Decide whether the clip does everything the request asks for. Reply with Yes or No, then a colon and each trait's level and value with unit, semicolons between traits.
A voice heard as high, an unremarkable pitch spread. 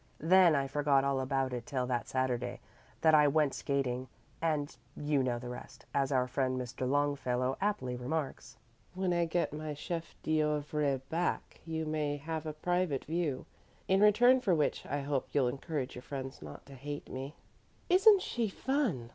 No: medium, 145 Hz; average, 3.6 semitones